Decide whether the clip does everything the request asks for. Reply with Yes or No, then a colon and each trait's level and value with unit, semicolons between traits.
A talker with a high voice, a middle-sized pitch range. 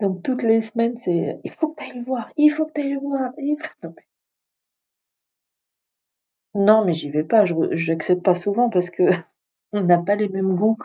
No: high, 215 Hz; wide, 6.1 semitones